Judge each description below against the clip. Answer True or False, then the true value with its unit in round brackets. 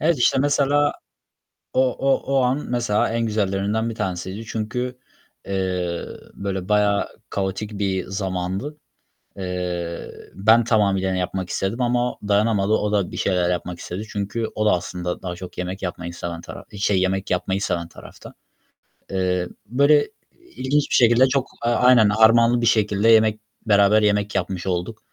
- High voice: False (105 Hz)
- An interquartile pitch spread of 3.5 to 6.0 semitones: True (4.0 semitones)